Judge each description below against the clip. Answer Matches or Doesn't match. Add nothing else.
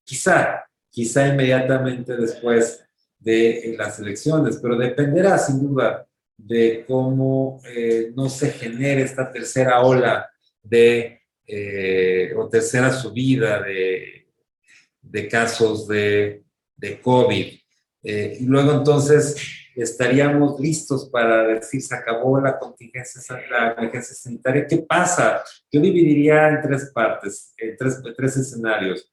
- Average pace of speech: Doesn't match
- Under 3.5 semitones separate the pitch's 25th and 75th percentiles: Matches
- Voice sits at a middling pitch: Doesn't match